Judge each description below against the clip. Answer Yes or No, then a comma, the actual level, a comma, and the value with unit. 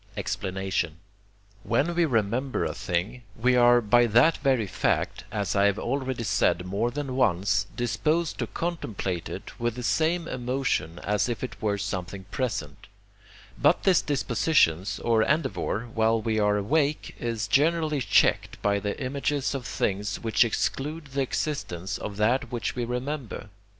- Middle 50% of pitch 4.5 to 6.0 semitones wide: Yes, average, 5.1 semitones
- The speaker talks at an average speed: Yes, average, 150 wpm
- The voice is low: Yes, low, 120 Hz